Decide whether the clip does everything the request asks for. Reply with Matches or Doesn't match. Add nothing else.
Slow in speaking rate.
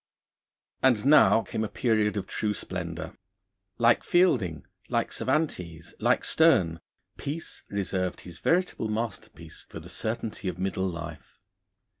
Matches